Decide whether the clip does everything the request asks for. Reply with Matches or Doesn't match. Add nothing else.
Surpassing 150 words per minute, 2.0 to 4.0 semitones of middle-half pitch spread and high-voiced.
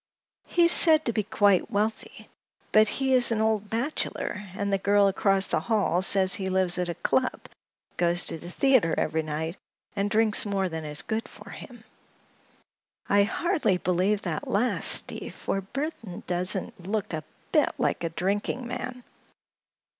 Matches